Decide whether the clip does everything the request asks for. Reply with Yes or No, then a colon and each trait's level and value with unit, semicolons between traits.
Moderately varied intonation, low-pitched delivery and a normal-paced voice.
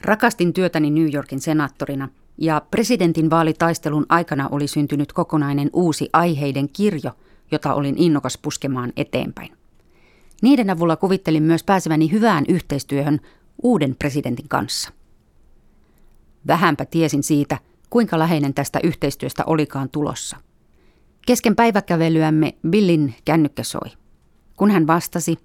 No: average, 3.2 semitones; medium, 155 Hz; average, 110 wpm